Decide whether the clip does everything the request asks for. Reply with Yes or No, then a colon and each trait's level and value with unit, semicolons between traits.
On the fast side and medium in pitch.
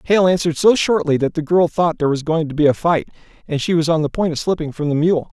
Yes: fast, 290 wpm; medium, 160 Hz